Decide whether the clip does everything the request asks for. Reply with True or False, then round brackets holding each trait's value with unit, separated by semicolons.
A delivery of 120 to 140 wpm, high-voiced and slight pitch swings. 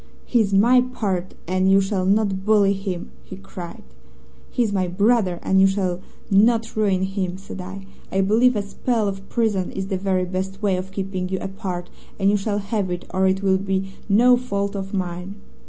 False (190 wpm; 195 Hz; 1.5 semitones)